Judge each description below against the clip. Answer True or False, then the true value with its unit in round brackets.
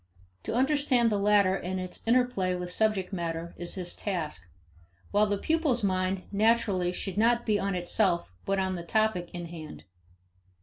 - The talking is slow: False (165 wpm)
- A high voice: True (195 Hz)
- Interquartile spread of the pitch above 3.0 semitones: True (3.5 semitones)